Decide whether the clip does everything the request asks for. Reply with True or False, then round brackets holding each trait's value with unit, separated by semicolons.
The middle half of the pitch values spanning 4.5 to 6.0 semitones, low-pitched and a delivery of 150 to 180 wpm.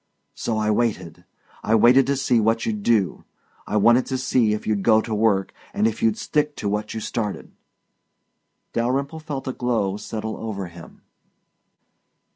False (2.8 semitones; 110 Hz; 165 wpm)